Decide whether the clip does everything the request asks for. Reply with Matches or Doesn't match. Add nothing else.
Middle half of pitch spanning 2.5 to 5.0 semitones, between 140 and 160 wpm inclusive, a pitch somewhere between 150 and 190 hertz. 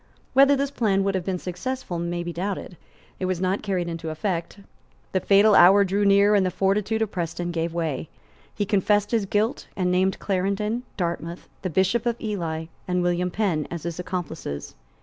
Doesn't match